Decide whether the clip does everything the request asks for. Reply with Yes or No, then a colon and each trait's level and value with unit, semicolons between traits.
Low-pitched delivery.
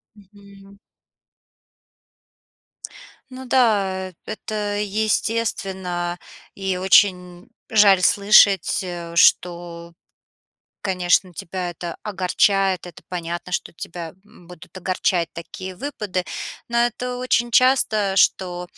No: high, 190 Hz